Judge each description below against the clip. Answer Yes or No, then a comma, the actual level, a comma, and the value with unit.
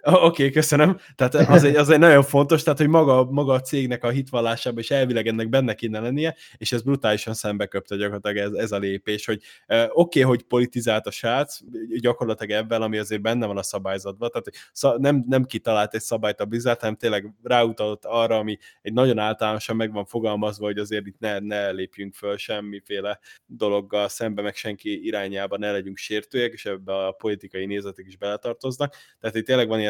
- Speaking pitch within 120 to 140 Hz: No, low, 110 Hz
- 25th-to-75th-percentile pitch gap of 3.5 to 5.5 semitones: Yes, average, 3.8 semitones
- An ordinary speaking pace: No, fast, 195 wpm